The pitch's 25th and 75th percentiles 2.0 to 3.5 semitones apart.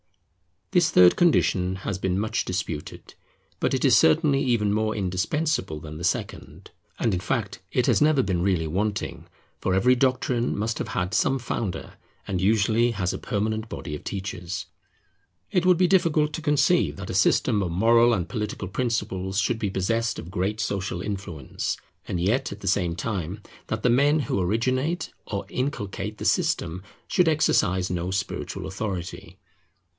No: average, 5.2 semitones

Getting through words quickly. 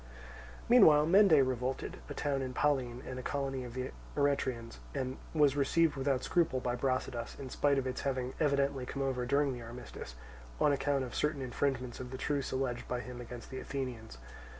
No: average, 185 wpm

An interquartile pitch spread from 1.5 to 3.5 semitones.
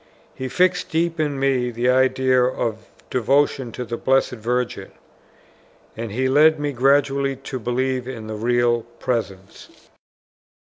Yes: narrow, 2.4 semitones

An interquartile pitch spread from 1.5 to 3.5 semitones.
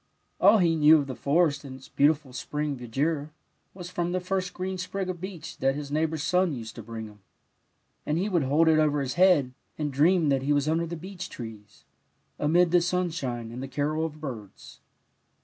No: average, 4.5 semitones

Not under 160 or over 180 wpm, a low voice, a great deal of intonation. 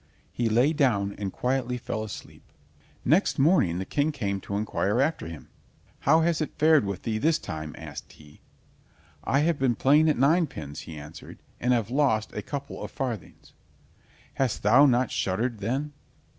Yes: average, 170 wpm; low, 125 Hz; wide, 6.4 semitones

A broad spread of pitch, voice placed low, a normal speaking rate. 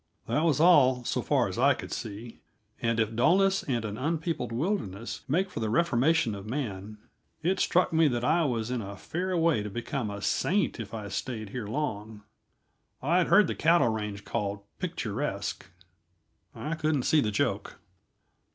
Yes: wide, 7.1 semitones; low, 120 Hz; average, 175 wpm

